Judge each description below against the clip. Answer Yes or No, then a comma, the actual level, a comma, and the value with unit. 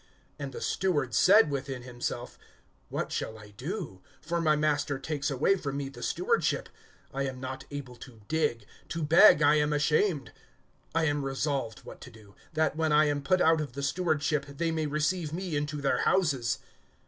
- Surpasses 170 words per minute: Yes, average, 185 wpm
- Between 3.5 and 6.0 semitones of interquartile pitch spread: No, average, 2.8 semitones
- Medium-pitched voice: Yes, medium, 145 Hz